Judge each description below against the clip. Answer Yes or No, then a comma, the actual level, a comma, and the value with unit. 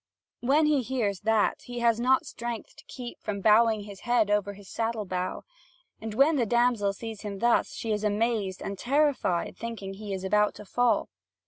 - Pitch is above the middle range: Yes, high, 220 Hz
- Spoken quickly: No, average, 190 wpm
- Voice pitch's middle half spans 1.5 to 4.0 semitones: Yes, average, 2.9 semitones